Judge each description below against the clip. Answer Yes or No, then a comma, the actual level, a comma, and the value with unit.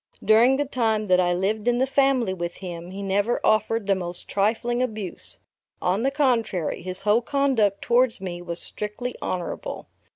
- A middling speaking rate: Yes, average, 170 wpm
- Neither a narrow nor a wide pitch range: Yes, average, 4.6 semitones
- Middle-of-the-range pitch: No, high, 215 Hz